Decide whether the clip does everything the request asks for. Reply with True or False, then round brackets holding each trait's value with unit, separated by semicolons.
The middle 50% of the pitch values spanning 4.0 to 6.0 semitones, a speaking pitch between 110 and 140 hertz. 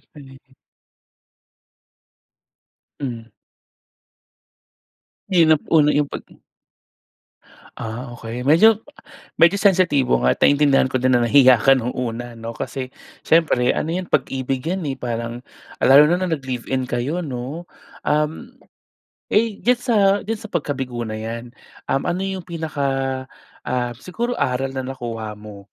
True (5.1 semitones; 135 Hz)